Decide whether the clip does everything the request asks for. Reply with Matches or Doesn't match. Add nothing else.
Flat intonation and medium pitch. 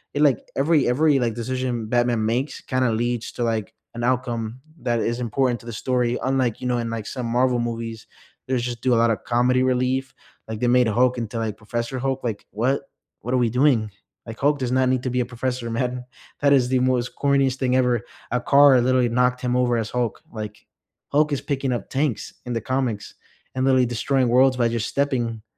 Doesn't match